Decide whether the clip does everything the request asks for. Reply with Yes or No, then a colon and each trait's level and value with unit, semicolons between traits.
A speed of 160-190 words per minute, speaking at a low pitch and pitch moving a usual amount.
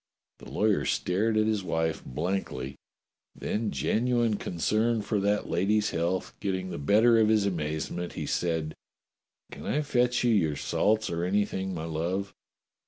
No: average, 150 wpm; low, 100 Hz; average, 4.3 semitones